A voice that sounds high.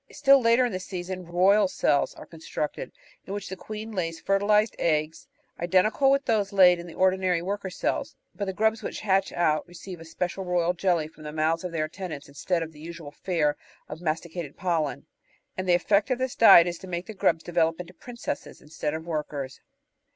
No: medium, 180 Hz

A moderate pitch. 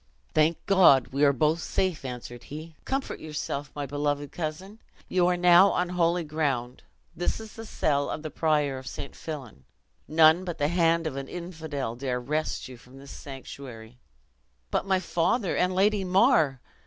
Yes: medium, 155 Hz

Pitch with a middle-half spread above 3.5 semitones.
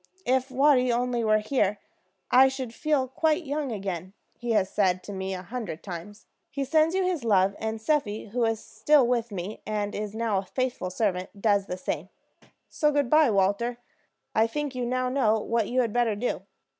Yes: average, 4.3 semitones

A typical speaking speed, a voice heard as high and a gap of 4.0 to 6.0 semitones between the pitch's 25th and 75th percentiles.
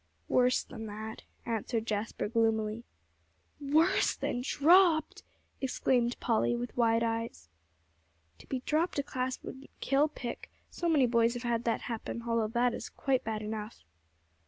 No: average, 145 wpm; high, 235 Hz; average, 2.9 semitones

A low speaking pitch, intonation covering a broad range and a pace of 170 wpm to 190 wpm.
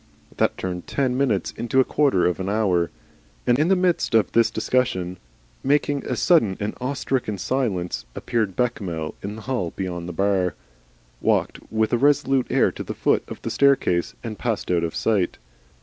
Yes: low, 110 Hz; wide, 6.2 semitones; average, 180 wpm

